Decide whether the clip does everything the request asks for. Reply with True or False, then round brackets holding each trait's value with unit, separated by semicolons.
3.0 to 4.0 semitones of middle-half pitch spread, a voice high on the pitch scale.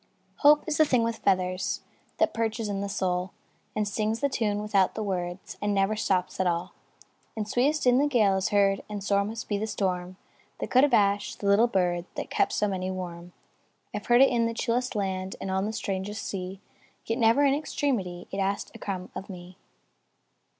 True (3.5 semitones; 200 Hz)